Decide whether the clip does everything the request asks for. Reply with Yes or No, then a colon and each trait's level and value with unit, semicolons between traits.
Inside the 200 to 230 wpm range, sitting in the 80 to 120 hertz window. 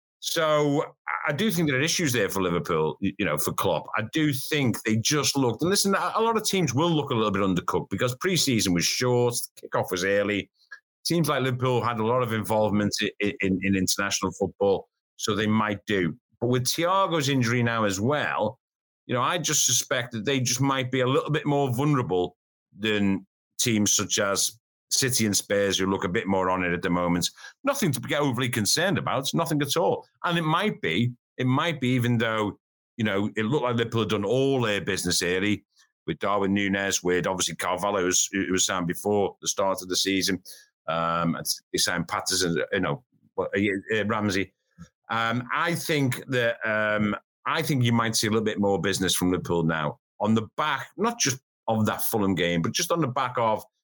Yes: fast, 205 wpm; low, 110 Hz